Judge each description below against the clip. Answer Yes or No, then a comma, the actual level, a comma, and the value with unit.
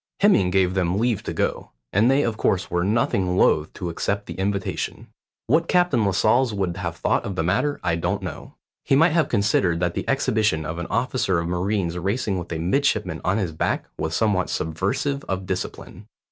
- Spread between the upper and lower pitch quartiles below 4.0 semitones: No, average, 4.7 semitones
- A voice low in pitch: Yes, very low, 95 Hz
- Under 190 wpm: No, average, 195 wpm